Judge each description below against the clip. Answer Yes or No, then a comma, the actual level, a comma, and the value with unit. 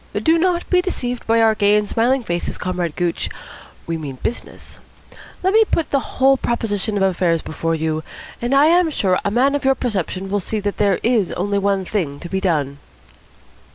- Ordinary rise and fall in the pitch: No, wide, 6.5 semitones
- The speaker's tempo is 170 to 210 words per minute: Yes, average, 195 wpm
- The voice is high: Yes, high, 205 Hz